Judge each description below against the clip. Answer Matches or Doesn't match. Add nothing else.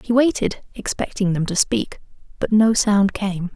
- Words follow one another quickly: Doesn't match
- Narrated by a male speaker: Doesn't match